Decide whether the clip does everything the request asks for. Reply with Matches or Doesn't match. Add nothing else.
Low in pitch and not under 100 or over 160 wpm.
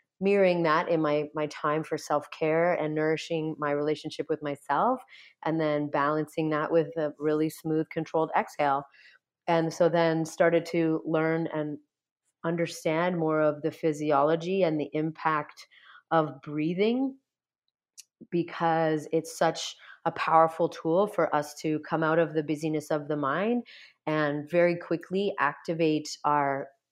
Doesn't match